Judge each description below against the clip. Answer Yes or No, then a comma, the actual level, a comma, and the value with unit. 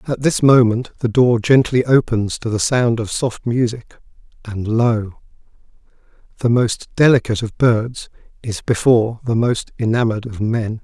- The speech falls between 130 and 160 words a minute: Yes, average, 150 wpm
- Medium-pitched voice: No, low, 115 Hz